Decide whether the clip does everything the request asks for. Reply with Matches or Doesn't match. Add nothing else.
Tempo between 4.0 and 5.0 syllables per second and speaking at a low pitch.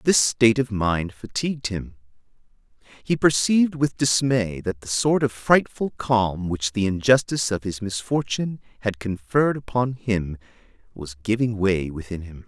Matches